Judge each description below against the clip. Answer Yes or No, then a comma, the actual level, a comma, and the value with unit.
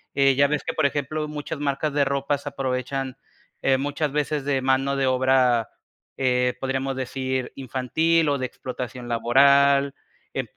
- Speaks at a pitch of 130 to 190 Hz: Yes, low, 135 Hz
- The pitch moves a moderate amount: No, narrow, 1.5 semitones